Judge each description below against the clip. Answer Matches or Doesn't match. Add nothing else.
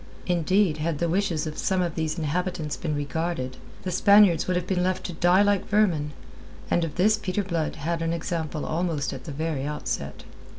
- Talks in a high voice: Doesn't match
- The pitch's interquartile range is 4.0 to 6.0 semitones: Doesn't match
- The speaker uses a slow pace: Doesn't match